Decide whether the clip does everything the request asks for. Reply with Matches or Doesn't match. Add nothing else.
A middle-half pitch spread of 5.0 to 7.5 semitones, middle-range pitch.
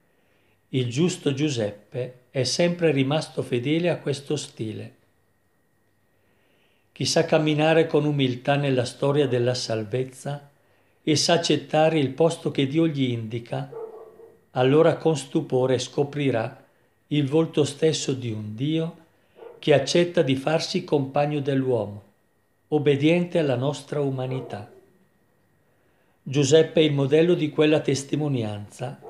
Doesn't match